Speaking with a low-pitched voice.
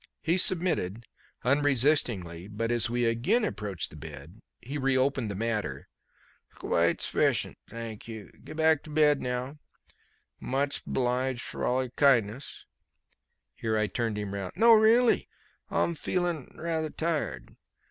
Yes: low, 125 Hz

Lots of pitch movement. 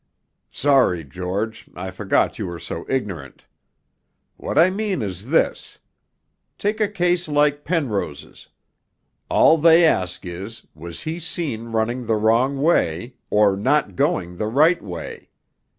Yes: wide, 8.8 semitones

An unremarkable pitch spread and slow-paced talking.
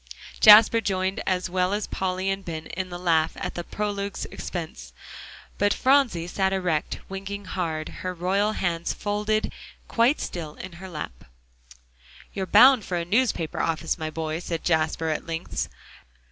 No: average, 3.3 semitones; average, 155 wpm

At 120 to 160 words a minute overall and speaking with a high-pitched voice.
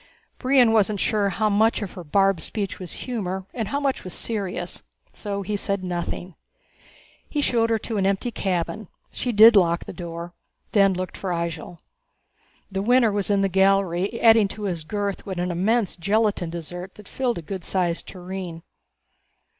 No: average, 175 wpm; high, 195 Hz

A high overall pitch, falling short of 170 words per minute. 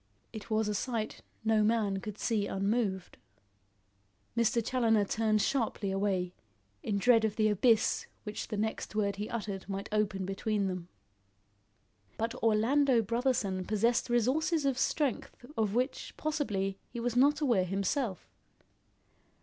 Yes: high, 215 Hz; slow, 135 wpm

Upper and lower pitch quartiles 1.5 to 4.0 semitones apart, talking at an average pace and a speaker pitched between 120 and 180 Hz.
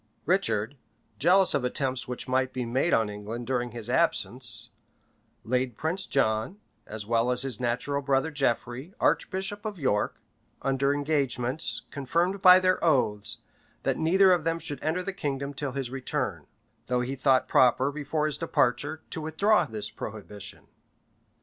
No: average, 4.6 semitones; average, 150 wpm; low, 135 Hz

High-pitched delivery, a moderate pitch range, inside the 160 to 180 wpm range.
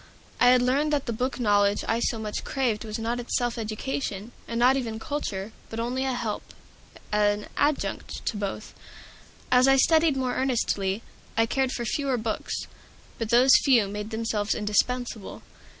Yes: high, 235 Hz; average, 3.3 semitones; average, 165 wpm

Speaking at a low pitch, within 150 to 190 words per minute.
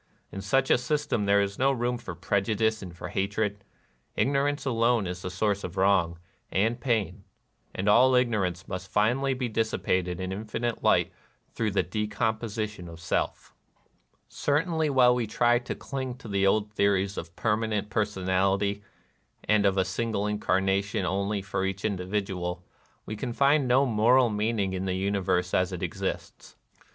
Yes: low, 105 Hz; average, 165 wpm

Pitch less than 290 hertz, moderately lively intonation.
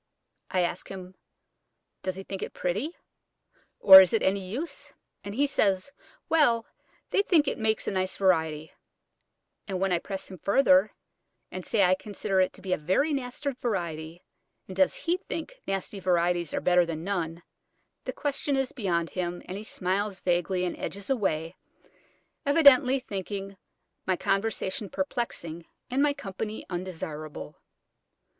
Yes: high, 190 Hz; average, 4.4 semitones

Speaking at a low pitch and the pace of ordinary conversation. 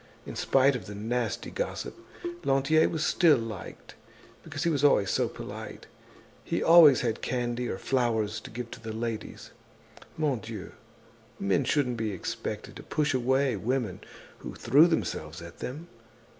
Yes: low, 125 Hz; average, 150 wpm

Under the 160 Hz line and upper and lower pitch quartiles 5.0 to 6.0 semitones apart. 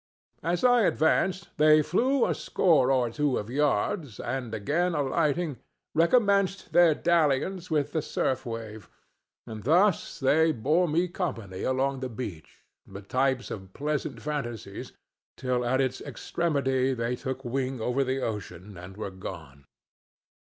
Yes: low, 135 Hz; wide, 5.5 semitones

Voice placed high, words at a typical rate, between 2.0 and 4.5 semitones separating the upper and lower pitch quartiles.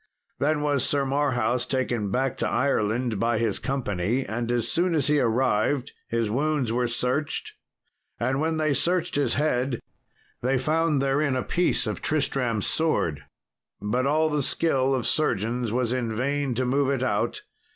No: low, 130 Hz; average, 160 wpm; average, 3.4 semitones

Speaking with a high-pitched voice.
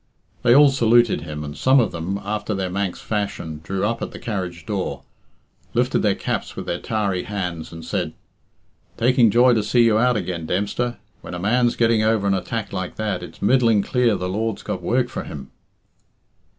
No: low, 105 Hz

